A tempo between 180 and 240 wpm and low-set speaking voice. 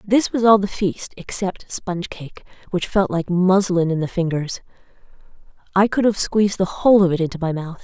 No: average, 200 wpm; medium, 185 Hz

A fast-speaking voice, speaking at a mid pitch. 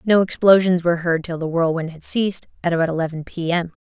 Yes: fast, 220 wpm; medium, 170 Hz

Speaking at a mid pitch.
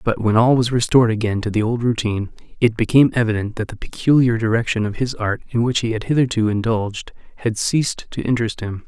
No: low, 115 Hz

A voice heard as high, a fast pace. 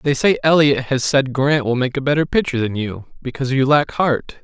No: low, 135 Hz; fast, 230 wpm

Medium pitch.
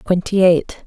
Yes: medium, 180 Hz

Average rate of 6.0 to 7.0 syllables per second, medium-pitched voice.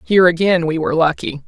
Yes: 6.8 syllables/s; medium, 170 Hz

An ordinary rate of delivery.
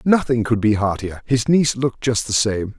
No: fast, 215 wpm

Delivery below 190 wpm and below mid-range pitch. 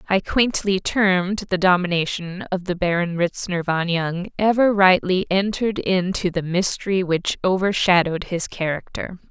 No: slow, 135 wpm; medium, 185 Hz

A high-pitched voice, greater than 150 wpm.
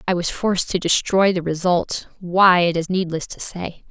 No: medium, 180 Hz; average, 200 wpm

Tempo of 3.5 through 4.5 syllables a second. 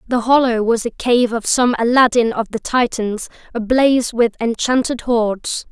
Yes: 4.4 syllables/s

